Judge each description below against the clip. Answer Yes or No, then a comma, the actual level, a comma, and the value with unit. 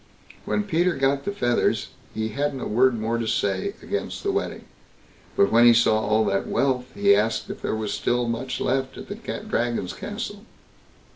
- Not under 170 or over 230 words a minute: Yes, average, 185 wpm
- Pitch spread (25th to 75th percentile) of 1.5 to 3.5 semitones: No, average, 4.0 semitones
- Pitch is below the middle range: Yes, low, 120 Hz